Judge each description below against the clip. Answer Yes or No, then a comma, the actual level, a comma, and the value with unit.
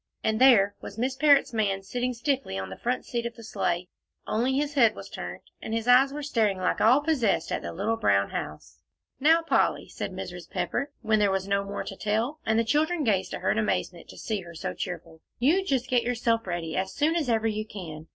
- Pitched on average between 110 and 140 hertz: No, high, 225 Hz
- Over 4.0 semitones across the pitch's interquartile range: Yes, average, 5.2 semitones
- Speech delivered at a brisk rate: Yes, fast, 230 wpm